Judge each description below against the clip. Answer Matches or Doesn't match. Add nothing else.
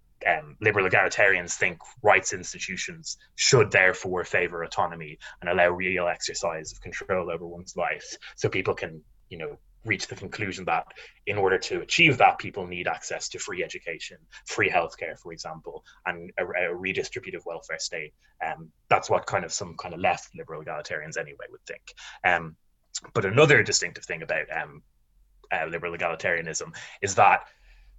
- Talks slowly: Doesn't match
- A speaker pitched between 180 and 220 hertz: Doesn't match